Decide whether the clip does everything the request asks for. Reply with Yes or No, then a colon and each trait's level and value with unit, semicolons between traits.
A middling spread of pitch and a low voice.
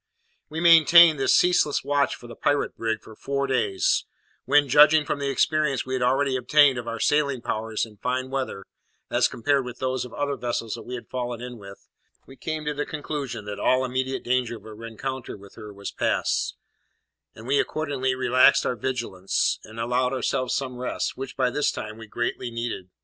Yes: average, 3.3 semitones; low, 130 Hz